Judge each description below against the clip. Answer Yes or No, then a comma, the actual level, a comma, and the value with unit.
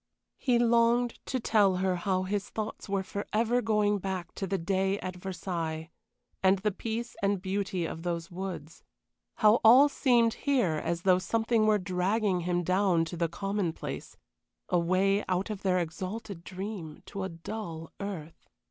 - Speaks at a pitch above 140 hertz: Yes, high, 190 Hz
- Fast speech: No, average, 155 wpm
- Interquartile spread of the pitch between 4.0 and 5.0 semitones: No, average, 3.3 semitones